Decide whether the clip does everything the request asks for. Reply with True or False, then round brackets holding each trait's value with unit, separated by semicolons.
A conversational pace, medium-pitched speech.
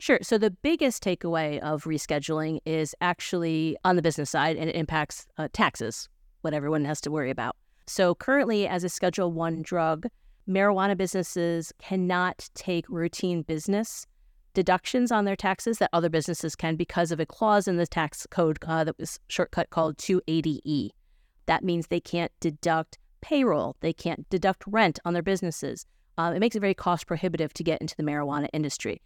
True (175 wpm; 170 Hz)